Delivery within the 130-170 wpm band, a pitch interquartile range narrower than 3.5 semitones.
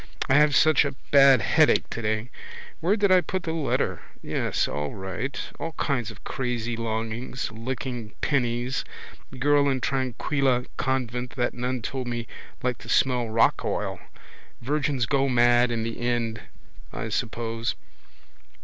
Yes: average, 140 wpm; average, 2.9 semitones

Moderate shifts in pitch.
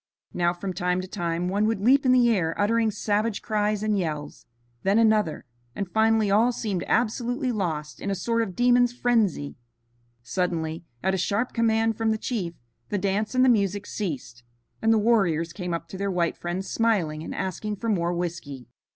Yes: average, 4.4 semitones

